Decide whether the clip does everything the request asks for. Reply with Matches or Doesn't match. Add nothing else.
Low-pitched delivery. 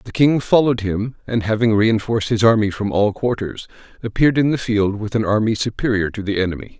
Matches